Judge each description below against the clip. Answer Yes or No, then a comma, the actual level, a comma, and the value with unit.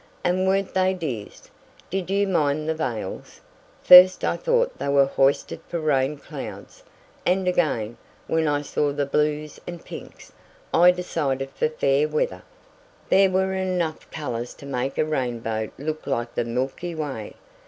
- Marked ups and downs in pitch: No, average, 5.0 semitones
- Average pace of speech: Yes, average, 155 wpm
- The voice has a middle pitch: Yes, medium, 150 Hz